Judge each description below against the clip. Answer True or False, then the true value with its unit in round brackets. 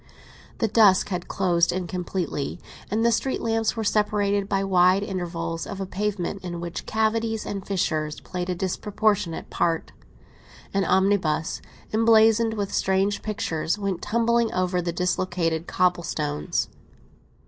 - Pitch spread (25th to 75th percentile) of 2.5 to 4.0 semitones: True (3.3 semitones)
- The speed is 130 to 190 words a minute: True (135 wpm)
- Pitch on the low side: False (190 Hz)